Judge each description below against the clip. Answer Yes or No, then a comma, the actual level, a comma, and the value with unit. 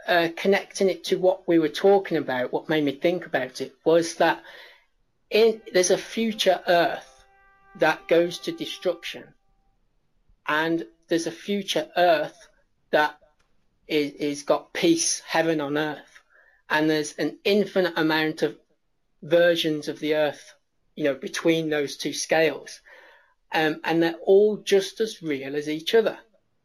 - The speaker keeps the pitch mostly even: No, average, 3.7 semitones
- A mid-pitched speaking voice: Yes, medium, 165 Hz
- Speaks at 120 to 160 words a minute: Yes, average, 145 wpm